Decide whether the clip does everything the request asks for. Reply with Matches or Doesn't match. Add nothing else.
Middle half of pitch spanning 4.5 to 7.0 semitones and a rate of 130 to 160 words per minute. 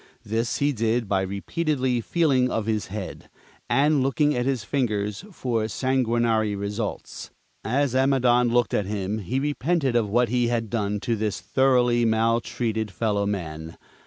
Doesn't match